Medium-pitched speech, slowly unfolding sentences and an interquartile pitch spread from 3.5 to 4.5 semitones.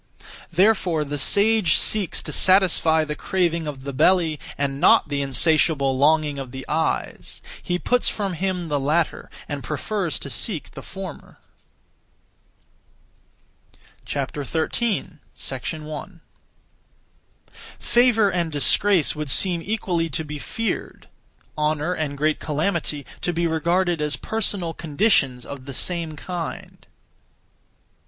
Yes: medium, 160 Hz; slow, 120 wpm; average, 3.9 semitones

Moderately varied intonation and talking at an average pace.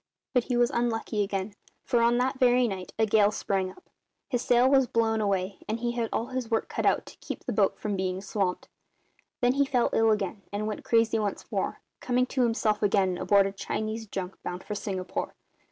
No: average, 3.3 semitones; fast, 210 wpm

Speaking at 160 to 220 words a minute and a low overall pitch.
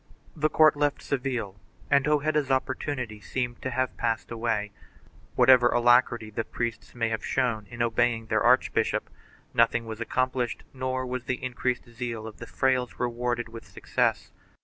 No: average, 150 wpm; low, 120 Hz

